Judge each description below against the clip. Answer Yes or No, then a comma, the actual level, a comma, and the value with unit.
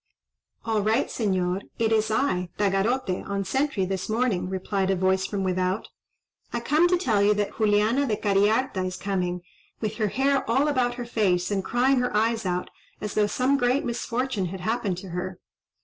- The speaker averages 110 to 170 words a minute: No, average, 180 wpm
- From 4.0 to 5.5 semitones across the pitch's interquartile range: Yes, average, 4.3 semitones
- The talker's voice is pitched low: No, high, 210 Hz